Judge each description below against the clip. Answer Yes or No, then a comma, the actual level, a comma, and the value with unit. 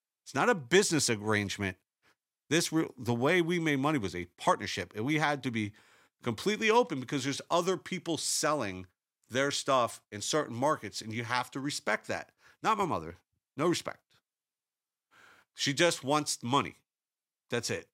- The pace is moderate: Yes, average, 160 wpm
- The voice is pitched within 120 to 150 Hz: Yes, medium, 140 Hz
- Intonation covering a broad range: Yes, wide, 6.6 semitones